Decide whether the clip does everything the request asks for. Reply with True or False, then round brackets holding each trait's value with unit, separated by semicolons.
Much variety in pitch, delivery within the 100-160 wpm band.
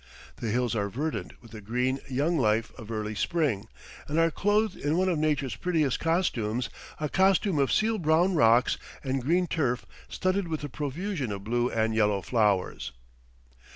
False (6.6 semitones; 170 wpm)